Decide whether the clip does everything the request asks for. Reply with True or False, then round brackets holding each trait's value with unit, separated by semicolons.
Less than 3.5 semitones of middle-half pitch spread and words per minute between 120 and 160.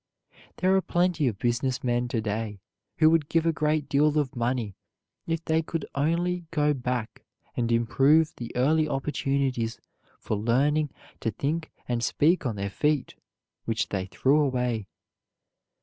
False (4.8 semitones; 150 wpm)